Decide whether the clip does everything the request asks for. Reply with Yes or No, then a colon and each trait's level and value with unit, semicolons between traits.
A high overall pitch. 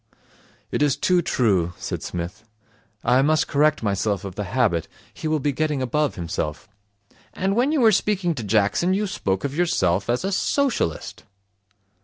No: low, 135 Hz